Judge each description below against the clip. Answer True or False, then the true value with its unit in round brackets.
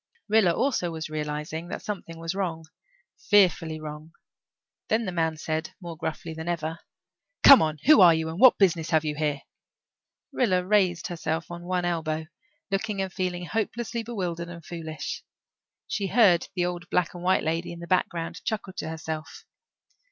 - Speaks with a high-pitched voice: False (170 Hz)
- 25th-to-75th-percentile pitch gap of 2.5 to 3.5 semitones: True (2.8 semitones)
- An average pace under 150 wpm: False (165 wpm)